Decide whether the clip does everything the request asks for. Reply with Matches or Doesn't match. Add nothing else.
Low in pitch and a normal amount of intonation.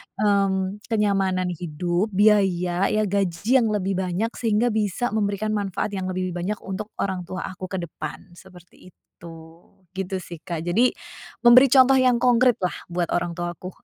Doesn't match